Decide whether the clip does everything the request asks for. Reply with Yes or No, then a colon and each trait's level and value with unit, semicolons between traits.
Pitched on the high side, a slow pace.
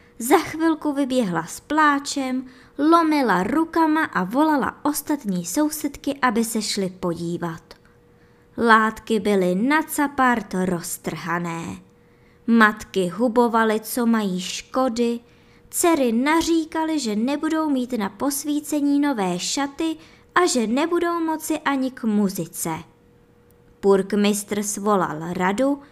Yes: very high, 250 Hz; slow, 100 wpm